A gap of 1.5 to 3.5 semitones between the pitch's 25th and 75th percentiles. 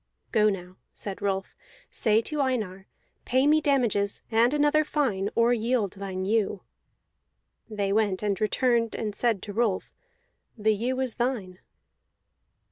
No: average, 4.0 semitones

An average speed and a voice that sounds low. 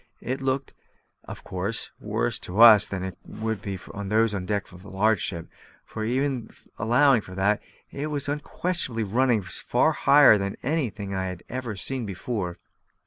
Yes: average, 170 wpm; low, 110 Hz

